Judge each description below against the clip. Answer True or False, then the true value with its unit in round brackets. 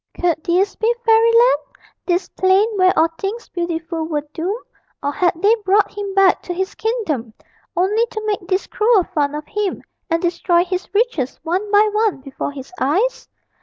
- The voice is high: True (375 Hz)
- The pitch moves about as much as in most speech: True (4.2 semitones)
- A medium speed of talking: True (170 wpm)